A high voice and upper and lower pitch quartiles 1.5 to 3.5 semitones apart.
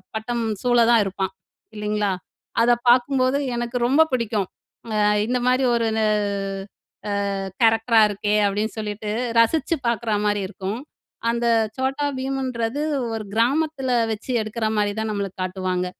Yes: high, 225 Hz; average, 3.2 semitones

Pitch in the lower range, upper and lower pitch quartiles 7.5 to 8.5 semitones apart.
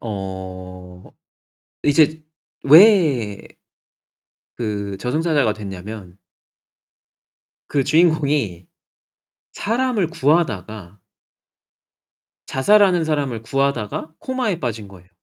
Yes: low, 125 Hz; wide, 8.2 semitones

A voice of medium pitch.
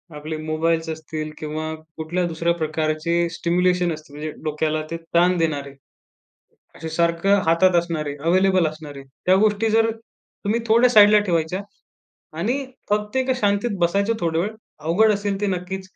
Yes: medium, 170 Hz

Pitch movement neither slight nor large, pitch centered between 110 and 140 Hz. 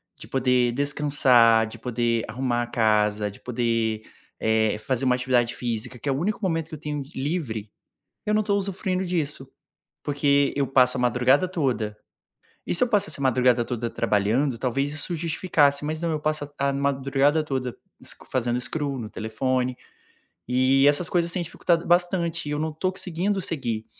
Yes: average, 4.7 semitones; low, 135 Hz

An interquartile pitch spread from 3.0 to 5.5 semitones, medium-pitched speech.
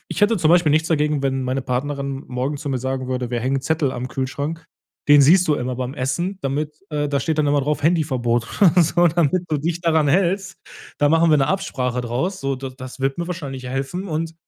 Yes: average, 3.8 semitones; medium, 145 Hz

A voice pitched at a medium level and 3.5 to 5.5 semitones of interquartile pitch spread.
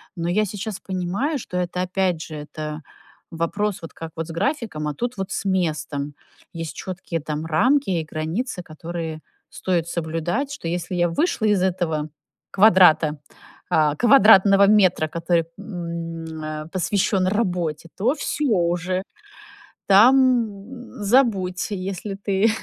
Yes: medium, 180 Hz; average, 3.8 semitones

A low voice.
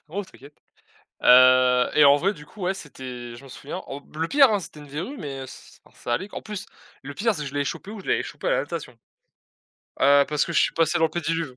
No: medium, 150 Hz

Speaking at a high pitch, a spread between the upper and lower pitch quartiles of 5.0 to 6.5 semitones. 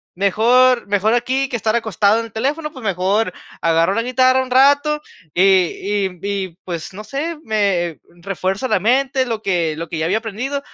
Yes: high, 220 Hz; average, 5.3 semitones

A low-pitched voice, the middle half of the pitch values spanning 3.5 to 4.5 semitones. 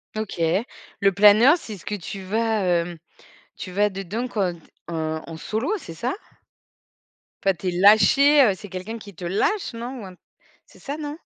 No: high, 205 Hz; average, 4.2 semitones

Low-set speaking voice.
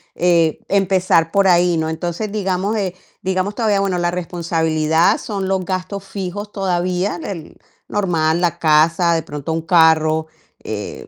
No: medium, 180 Hz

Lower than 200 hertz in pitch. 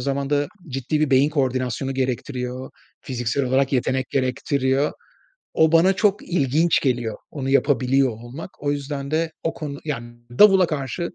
Yes: medium, 140 Hz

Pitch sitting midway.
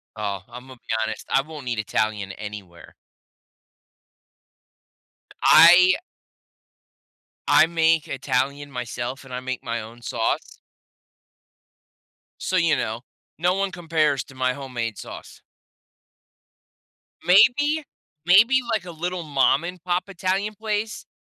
Yes: medium, 145 Hz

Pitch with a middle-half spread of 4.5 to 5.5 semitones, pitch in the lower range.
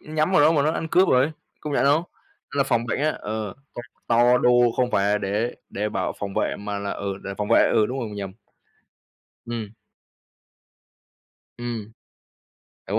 Yes: average, 5.2 semitones; low, 115 Hz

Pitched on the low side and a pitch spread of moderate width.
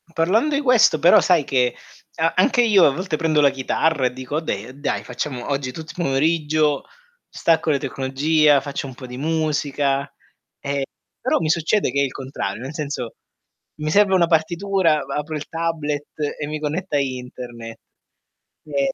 No: medium, 150 Hz; average, 3.2 semitones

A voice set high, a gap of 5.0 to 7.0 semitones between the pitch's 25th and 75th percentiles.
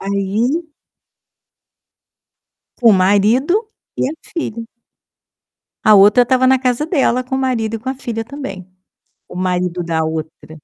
Yes: high, 225 Hz; wide, 5.5 semitones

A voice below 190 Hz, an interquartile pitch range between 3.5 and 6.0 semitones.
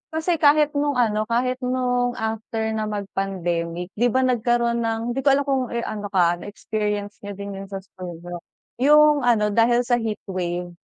No: high, 225 Hz; average, 4.0 semitones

